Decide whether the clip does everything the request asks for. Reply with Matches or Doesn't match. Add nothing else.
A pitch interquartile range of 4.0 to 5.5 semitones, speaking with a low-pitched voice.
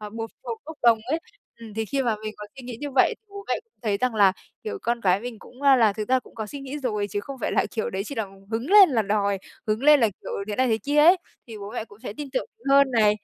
Doesn't match